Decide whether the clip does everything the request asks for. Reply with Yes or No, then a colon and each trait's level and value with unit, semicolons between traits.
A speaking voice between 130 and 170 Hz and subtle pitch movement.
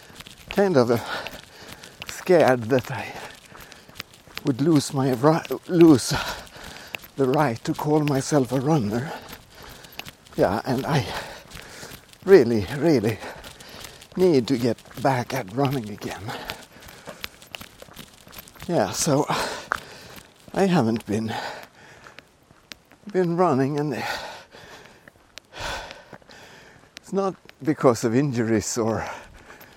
No: low, 135 Hz; average, 4.6 semitones